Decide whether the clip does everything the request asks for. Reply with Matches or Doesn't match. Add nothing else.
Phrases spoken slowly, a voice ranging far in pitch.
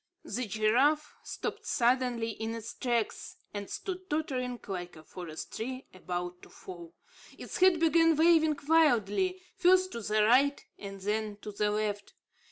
Doesn't match